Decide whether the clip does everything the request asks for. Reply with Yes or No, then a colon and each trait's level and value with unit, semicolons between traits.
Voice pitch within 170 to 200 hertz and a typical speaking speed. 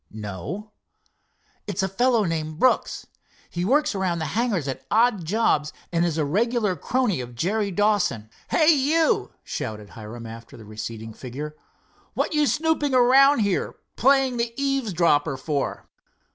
Yes: high, 190 Hz; average, 145 wpm